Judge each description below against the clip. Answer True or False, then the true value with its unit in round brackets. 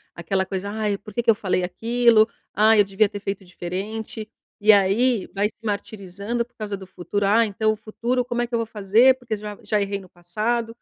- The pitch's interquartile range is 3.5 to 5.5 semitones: False (2.6 semitones)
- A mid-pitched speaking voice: False (210 Hz)